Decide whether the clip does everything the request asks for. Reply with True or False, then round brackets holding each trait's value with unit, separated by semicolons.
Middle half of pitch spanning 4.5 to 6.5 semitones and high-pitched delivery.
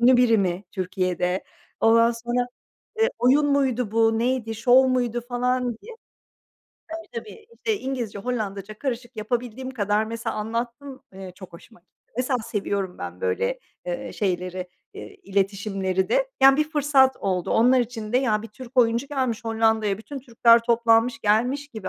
False (3.4 semitones; 230 Hz)